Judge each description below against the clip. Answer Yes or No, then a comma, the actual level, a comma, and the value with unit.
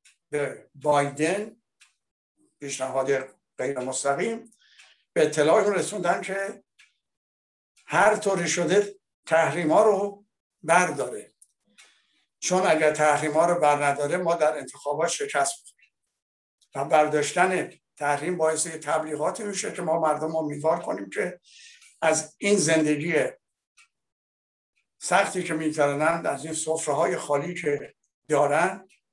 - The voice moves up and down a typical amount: Yes, average, 4.2 semitones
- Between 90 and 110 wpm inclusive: Yes, slow, 105 wpm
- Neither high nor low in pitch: Yes, medium, 160 Hz